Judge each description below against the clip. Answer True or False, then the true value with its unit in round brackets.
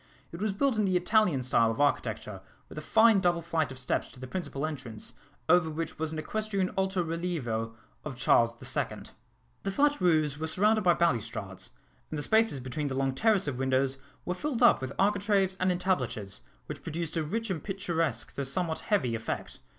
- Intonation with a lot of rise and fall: True (6.4 semitones)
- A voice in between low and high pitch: True (160 Hz)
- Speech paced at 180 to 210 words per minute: True (195 wpm)